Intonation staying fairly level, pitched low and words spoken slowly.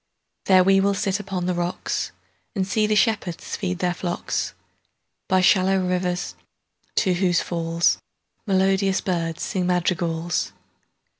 No: narrow, 1.6 semitones; medium, 185 Hz; slow, 115 wpm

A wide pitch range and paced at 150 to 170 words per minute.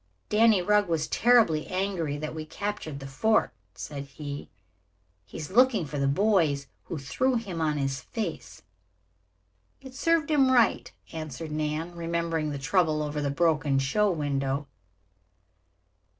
No: wide, 6.1 semitones; average, 140 wpm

